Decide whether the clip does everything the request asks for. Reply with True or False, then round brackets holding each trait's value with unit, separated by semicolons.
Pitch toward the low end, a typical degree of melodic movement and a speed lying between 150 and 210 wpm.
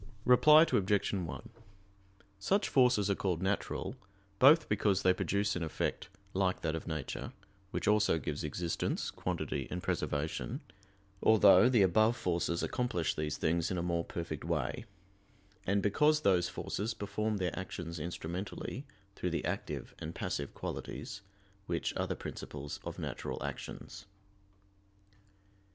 False (95 Hz; 3.9 semitones; 135 wpm)